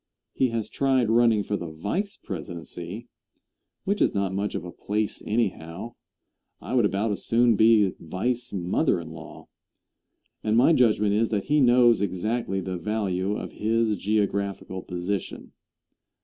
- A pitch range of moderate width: Yes, average, 3.7 semitones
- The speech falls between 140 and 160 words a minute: Yes, average, 150 wpm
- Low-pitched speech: Yes, low, 105 Hz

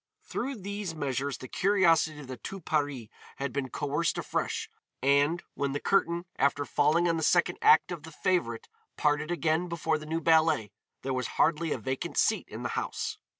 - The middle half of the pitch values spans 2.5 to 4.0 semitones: Yes, average, 3.2 semitones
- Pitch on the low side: No, medium, 155 Hz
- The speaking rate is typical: Yes, average, 185 wpm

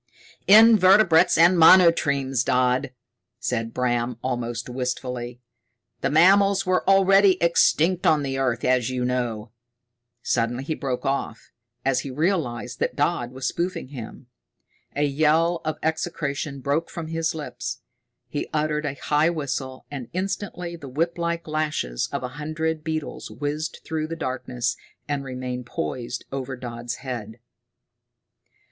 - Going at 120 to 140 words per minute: Yes, slow, 135 wpm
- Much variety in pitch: No, average, 4.7 semitones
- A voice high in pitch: No, medium, 140 Hz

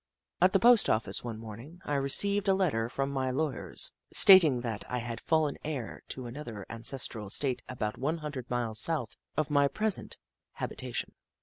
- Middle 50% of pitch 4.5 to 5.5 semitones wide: Yes, average, 5.1 semitones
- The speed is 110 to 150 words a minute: No, average, 175 wpm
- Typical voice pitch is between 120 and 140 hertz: Yes, low, 135 Hz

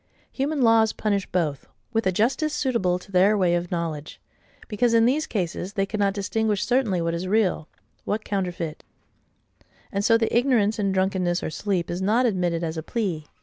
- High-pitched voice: Yes, high, 195 Hz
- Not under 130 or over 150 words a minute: No, average, 175 wpm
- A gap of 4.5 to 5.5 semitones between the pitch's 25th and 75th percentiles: No, average, 4.1 semitones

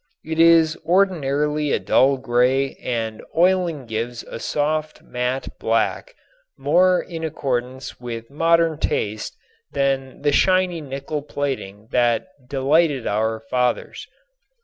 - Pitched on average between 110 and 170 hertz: Yes, medium, 140 Hz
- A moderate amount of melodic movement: Yes, average, 4.7 semitones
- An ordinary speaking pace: No, slow, 115 wpm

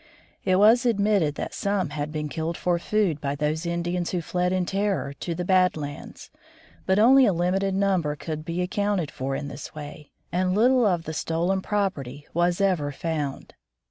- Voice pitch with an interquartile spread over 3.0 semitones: Yes, average, 4.3 semitones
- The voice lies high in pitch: No, medium, 175 Hz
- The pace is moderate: Yes, average, 180 wpm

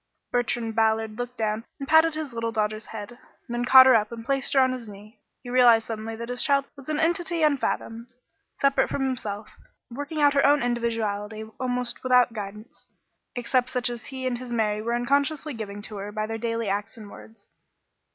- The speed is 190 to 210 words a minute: Yes, average, 195 wpm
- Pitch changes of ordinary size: Yes, average, 3.1 semitones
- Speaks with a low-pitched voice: No, high, 240 Hz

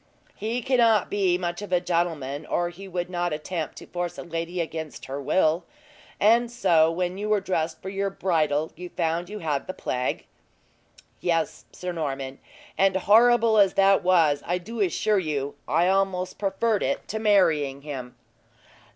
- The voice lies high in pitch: No, medium, 175 Hz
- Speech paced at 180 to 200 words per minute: No, average, 170 wpm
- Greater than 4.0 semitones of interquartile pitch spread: No, average, 3.7 semitones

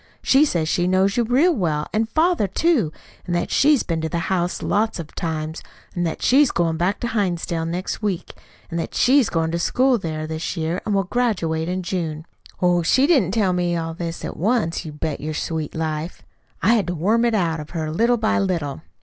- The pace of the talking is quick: Yes, fast, 220 wpm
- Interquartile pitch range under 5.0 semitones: No, average, 5.3 semitones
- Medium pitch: Yes, medium, 175 Hz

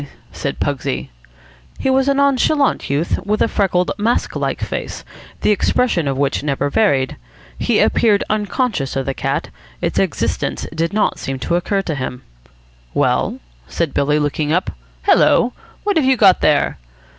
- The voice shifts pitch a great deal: Yes, wide, 8.1 semitones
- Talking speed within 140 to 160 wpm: Yes, average, 155 wpm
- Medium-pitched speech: Yes, medium, 180 Hz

